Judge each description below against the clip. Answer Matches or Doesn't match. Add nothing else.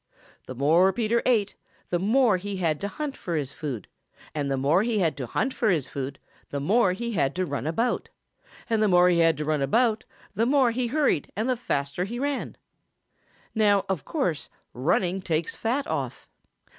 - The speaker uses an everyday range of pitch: Doesn't match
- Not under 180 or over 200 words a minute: Matches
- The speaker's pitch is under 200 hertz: Matches